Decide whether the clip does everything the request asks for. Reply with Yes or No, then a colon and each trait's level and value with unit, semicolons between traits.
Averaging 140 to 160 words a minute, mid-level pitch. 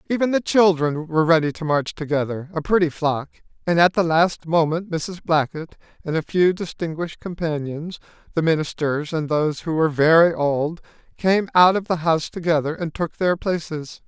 No: average, 175 wpm; medium, 165 Hz